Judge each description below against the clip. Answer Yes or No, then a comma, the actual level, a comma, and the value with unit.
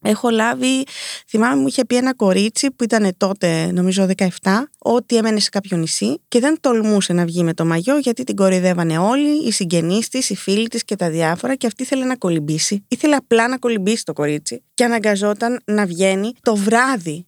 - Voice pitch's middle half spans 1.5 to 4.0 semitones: No, average, 4.8 semitones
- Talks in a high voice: Yes, high, 215 Hz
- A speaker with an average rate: No, fast, 195 wpm